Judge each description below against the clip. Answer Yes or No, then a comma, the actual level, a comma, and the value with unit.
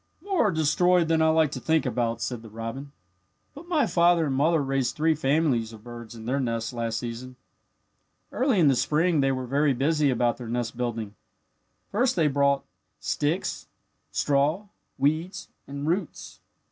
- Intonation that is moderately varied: Yes, average, 5.0 semitones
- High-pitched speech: No, medium, 140 Hz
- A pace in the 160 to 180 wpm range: Yes, average, 170 wpm